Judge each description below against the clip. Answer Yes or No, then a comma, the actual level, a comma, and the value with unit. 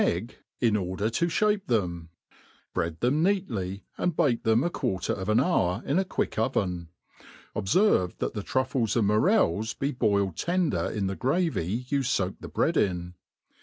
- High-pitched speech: No, low, 110 Hz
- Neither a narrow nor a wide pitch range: No, wide, 7.5 semitones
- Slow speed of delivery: No, average, 170 wpm